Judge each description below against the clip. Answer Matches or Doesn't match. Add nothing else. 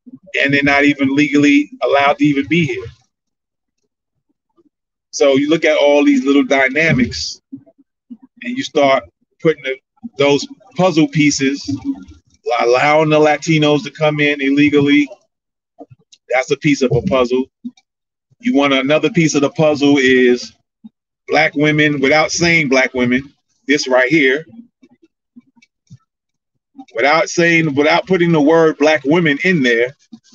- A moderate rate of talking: Doesn't match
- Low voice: Doesn't match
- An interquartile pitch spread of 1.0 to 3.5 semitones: Doesn't match